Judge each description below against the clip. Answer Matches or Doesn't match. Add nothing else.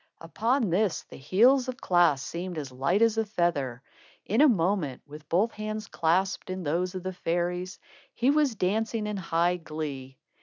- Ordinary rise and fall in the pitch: Matches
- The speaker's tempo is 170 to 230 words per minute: Matches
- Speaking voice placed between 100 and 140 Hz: Doesn't match